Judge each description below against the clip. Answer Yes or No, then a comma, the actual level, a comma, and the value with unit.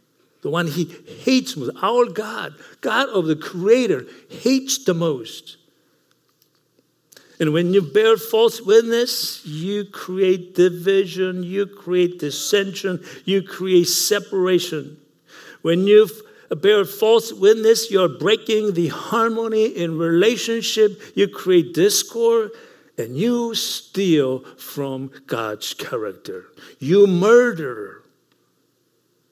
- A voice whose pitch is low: No, high, 200 Hz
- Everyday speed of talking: No, slow, 105 wpm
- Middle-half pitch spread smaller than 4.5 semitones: No, average, 4.8 semitones